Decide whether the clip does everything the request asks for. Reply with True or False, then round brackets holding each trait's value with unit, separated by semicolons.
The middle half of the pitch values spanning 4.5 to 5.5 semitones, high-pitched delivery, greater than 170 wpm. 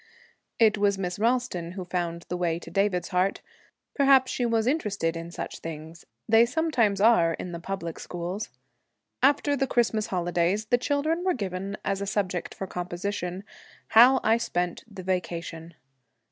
False (4.8 semitones; 195 Hz; 160 wpm)